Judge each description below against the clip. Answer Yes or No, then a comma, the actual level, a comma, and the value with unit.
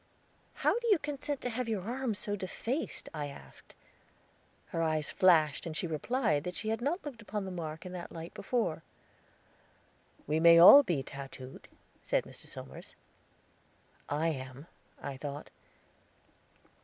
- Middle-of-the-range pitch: Yes, medium, 175 Hz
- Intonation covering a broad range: Yes, wide, 7.1 semitones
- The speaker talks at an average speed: Yes, average, 150 wpm